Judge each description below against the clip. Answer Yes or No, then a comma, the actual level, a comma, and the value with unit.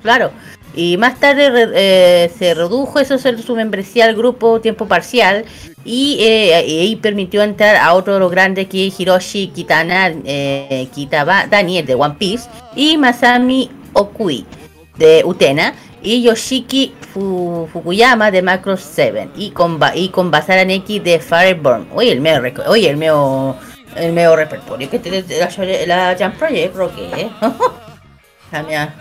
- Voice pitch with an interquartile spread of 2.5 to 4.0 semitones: No, average, 5.2 semitones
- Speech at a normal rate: Yes, average, 145 wpm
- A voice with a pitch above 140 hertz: Yes, high, 190 Hz